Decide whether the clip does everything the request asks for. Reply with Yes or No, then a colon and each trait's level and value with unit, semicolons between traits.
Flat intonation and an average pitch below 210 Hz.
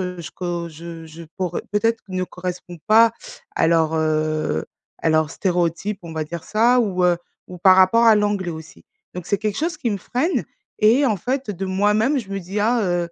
No: average, 4.0 semitones; medium, 185 Hz